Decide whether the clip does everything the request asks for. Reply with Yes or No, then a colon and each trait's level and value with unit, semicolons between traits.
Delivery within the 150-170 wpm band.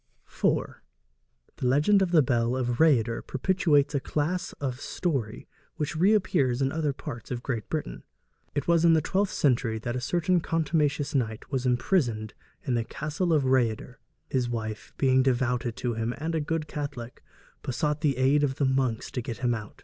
No: average, 180 wpm